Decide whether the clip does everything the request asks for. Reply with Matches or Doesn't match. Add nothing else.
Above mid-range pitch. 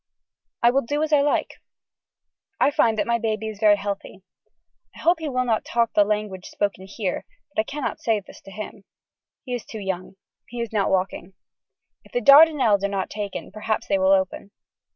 Matches